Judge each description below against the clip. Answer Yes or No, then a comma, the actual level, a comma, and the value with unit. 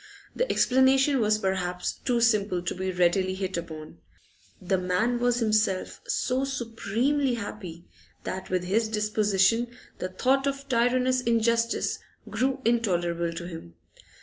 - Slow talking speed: Yes, slow, 130 wpm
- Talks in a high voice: Yes, high, 215 Hz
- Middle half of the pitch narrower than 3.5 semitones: No, average, 5.0 semitones